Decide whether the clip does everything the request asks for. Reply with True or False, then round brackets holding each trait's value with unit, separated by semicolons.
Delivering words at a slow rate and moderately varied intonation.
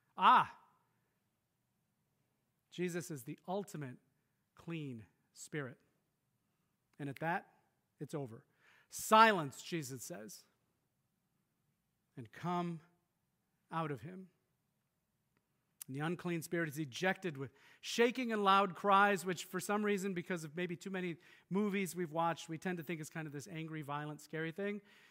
True (130 wpm; 3.3 semitones)